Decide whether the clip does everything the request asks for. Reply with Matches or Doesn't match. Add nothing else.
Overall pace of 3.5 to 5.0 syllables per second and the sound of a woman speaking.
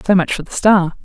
Doesn't match